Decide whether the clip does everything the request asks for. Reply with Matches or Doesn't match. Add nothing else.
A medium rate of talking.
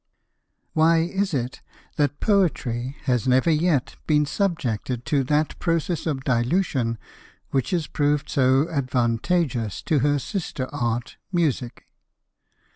Doesn't match